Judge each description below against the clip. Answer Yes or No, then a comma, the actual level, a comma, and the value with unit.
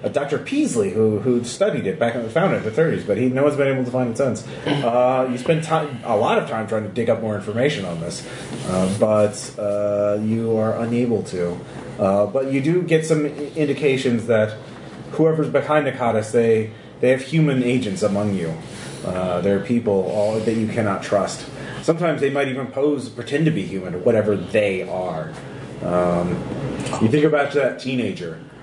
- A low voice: Yes, low, 120 Hz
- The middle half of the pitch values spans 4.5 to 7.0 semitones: Yes, average, 5.2 semitones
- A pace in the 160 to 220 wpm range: Yes, average, 195 wpm